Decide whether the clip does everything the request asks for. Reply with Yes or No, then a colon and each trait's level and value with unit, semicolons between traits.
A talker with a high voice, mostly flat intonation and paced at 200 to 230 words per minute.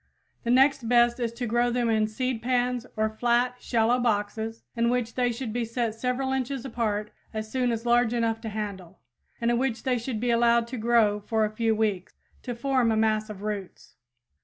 Yes: high, 235 Hz; narrow, 2.1 semitones; fast, 205 wpm